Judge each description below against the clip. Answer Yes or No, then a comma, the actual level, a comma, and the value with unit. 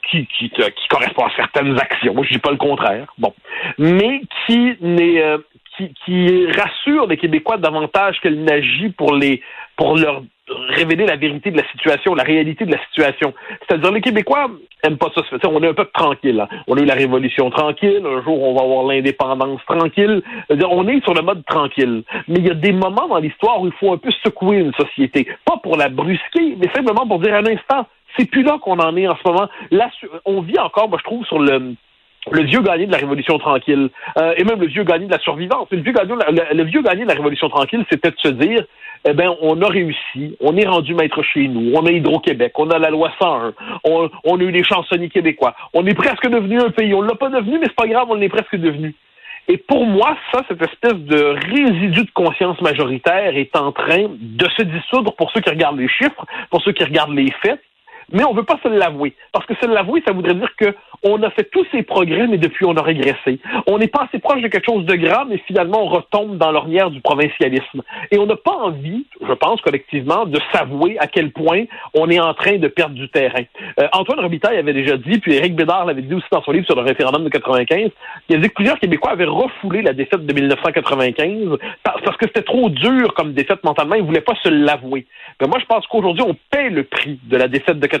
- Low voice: No, medium, 175 Hz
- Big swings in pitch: Yes, wide, 6.5 semitones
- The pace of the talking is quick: Yes, fast, 235 wpm